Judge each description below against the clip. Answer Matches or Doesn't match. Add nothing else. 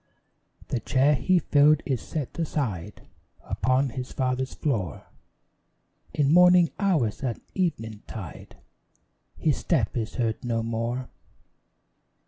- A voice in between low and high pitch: Doesn't match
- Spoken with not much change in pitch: Doesn't match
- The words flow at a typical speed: Doesn't match